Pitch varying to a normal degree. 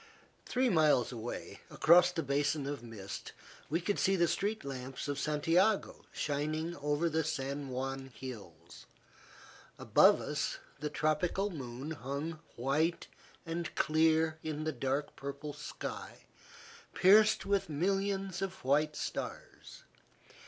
Yes: average, 3.7 semitones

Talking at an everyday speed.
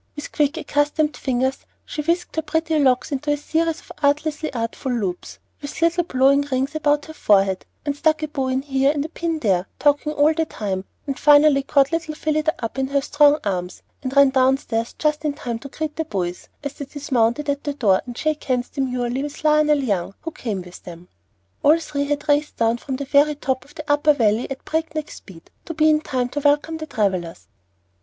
No: fast, 210 wpm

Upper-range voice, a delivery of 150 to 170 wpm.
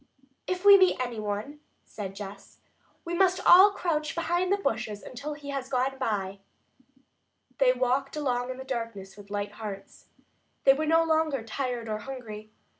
Yes: very high, 255 Hz; average, 160 wpm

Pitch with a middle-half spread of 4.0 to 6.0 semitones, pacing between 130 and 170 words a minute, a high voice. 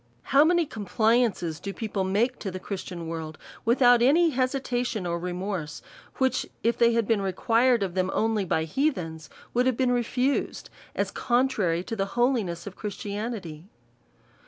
Yes: average, 5.2 semitones; average, 160 wpm; high, 220 Hz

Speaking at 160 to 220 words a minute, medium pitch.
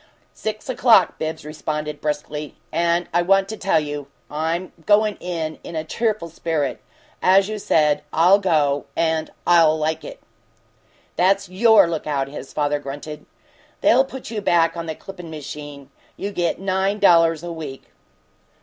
No: average, 150 wpm; medium, 165 Hz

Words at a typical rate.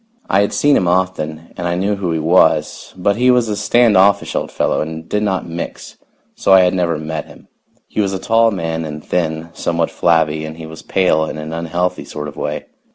No: fast, 220 wpm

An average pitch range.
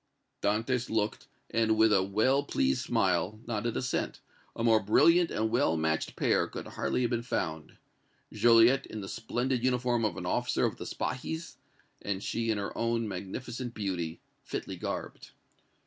Yes: average, 3.2 semitones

